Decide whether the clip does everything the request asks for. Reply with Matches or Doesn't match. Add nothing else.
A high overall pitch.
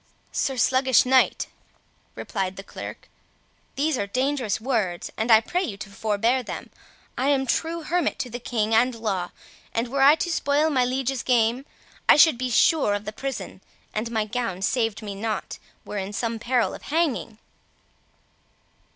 Matches